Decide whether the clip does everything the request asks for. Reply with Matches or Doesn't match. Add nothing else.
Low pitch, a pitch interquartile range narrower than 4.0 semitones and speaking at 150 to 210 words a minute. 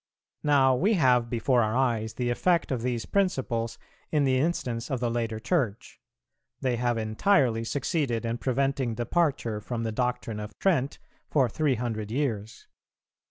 Matches